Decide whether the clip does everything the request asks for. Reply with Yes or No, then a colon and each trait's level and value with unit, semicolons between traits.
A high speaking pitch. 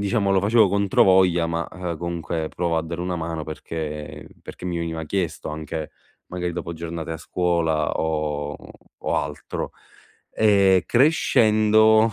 No: very low, 85 Hz